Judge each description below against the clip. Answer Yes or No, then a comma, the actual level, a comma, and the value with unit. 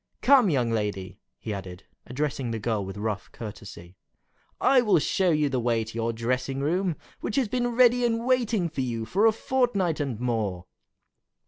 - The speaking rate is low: No, average, 180 wpm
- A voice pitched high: No, low, 135 Hz